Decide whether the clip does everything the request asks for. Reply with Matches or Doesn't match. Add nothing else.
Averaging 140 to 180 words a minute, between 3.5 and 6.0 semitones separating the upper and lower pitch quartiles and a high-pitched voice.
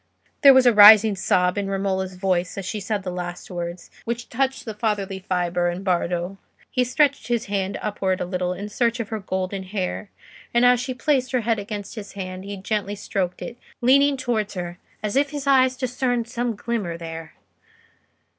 Doesn't match